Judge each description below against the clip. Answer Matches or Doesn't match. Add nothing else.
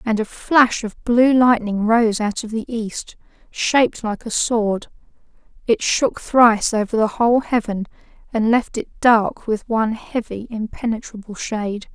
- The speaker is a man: Doesn't match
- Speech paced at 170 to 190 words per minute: Doesn't match